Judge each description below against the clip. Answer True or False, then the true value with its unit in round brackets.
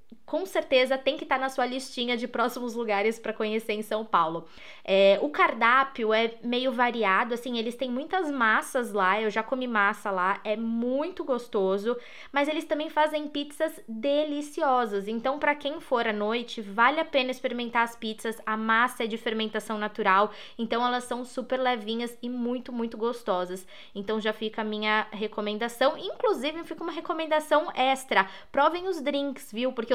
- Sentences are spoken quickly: False (170 wpm)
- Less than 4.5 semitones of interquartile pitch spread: True (3.8 semitones)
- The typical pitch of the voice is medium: False (240 Hz)